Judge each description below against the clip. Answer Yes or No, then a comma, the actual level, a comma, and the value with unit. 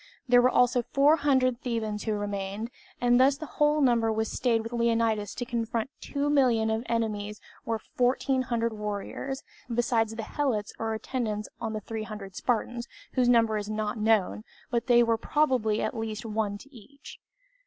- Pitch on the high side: Yes, high, 230 Hz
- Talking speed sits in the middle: Yes, average, 165 wpm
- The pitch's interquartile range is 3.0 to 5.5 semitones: No, narrow, 2.5 semitones